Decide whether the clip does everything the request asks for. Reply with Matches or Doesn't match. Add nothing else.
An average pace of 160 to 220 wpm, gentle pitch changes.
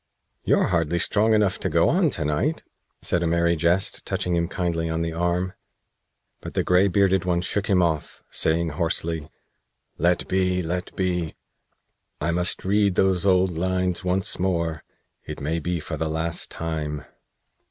Matches